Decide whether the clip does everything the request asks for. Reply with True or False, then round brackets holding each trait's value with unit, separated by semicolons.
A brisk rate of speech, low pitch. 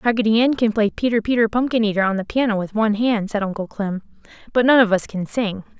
False (240 wpm; 215 Hz)